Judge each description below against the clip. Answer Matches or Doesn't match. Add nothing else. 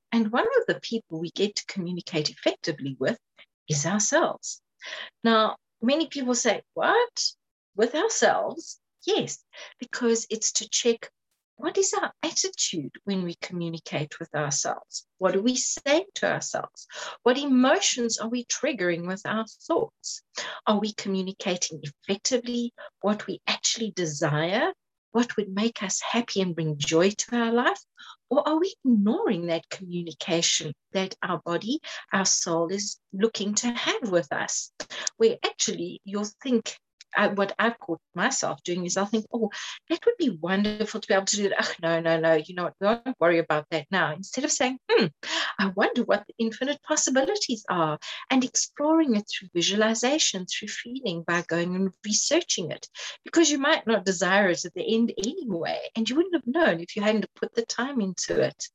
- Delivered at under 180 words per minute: Matches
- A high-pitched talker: Matches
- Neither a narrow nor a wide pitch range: Doesn't match